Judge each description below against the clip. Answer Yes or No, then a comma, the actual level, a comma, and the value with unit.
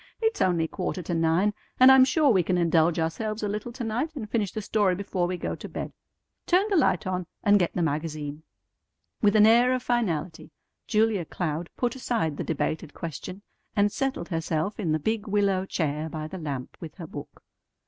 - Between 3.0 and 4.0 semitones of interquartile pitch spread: No, average, 5.2 semitones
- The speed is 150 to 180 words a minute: No, average, 200 wpm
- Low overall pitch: No, medium, 185 Hz